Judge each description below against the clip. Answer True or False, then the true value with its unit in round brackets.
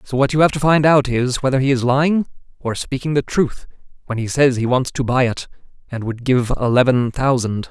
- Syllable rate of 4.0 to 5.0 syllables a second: False (5.4 syllables/s)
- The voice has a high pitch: False (130 Hz)